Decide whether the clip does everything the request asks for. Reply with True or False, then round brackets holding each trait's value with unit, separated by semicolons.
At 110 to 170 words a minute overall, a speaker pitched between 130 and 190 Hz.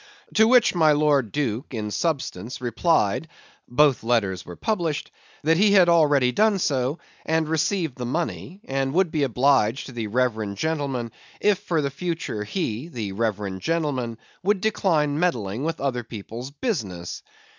True (155 wpm; 140 Hz)